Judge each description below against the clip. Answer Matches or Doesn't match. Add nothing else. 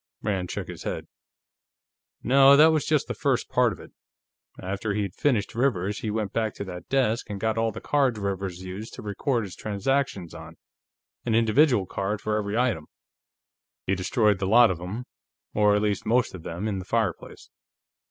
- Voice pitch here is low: Matches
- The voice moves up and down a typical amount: Matches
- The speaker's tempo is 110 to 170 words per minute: Doesn't match